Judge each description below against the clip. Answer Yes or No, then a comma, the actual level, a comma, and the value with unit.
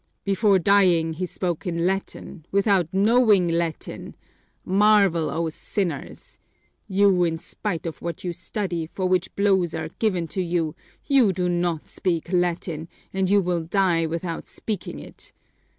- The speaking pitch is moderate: Yes, medium, 180 Hz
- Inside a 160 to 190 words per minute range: No, average, 145 wpm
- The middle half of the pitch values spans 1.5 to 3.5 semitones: Yes, average, 2.9 semitones